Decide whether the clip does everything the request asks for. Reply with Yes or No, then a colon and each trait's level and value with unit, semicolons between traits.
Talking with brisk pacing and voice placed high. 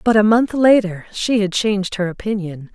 No: average, 195 wpm; high, 205 Hz